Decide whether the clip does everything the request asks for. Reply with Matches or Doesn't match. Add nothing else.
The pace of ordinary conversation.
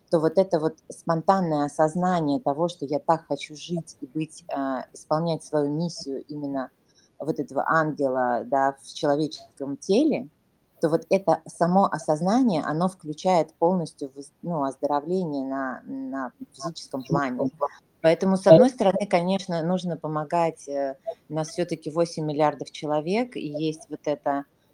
Matches